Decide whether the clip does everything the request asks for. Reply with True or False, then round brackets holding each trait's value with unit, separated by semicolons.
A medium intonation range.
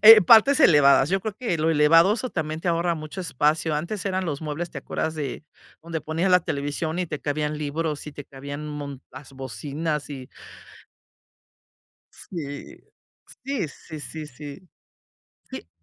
True (3.0 semitones)